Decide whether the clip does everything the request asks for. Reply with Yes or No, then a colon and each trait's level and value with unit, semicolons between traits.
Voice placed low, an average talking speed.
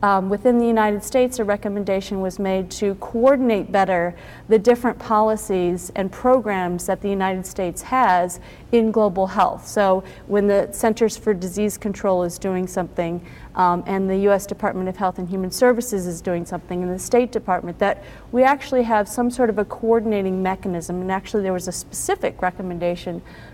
No: high, 200 Hz; average, 175 wpm